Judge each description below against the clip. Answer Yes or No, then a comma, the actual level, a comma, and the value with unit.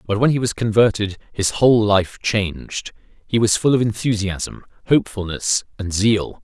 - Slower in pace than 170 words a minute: Yes, average, 160 wpm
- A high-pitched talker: No, low, 105 Hz